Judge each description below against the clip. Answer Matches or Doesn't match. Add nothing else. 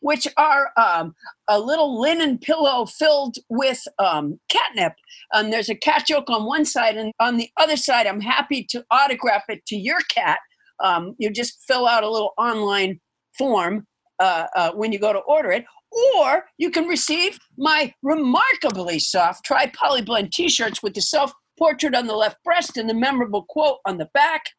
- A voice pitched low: Doesn't match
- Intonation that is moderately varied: Doesn't match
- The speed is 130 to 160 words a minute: Doesn't match